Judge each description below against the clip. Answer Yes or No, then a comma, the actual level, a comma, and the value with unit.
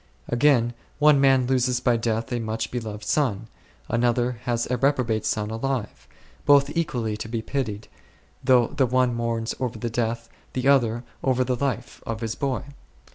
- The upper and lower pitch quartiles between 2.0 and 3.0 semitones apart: Yes, narrow, 2.4 semitones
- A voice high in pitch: No, low, 120 Hz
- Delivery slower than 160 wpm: No, average, 165 wpm